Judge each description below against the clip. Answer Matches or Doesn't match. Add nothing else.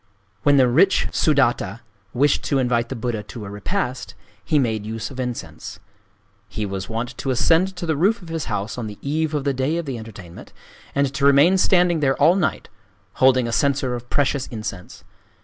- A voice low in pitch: Matches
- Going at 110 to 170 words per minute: Doesn't match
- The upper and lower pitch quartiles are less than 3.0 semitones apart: Doesn't match